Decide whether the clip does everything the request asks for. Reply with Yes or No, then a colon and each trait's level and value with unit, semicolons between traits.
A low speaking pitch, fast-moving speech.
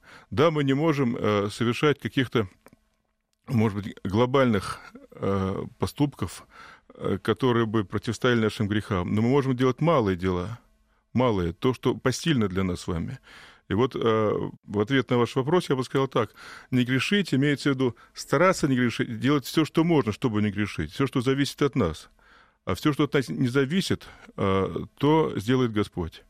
Yes: low, 125 Hz; fast, 170 wpm